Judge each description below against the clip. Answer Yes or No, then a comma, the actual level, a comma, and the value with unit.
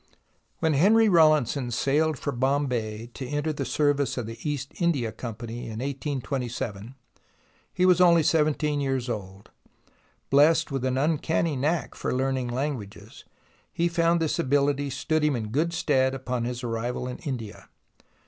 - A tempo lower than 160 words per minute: Yes, average, 150 wpm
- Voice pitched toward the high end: No, low, 135 Hz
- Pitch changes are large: No, average, 4.0 semitones